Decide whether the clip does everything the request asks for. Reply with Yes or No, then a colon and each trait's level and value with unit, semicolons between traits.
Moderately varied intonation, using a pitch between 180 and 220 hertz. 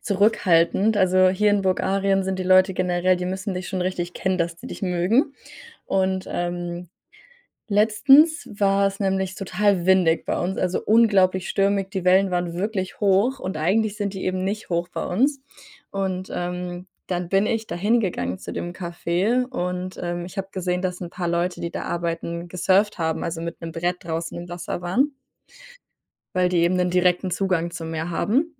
No: narrow, 2.1 semitones; medium, 185 Hz